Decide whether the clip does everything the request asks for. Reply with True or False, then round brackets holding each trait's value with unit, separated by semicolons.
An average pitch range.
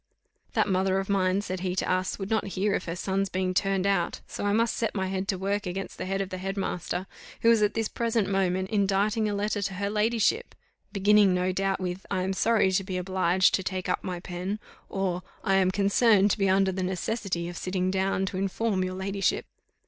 False (1.5 semitones)